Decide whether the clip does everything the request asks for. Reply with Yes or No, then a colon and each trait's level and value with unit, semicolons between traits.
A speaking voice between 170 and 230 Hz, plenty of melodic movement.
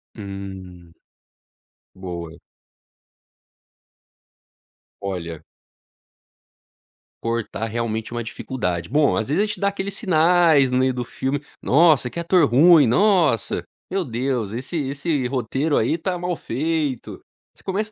No: low, 130 Hz; wide, 7.1 semitones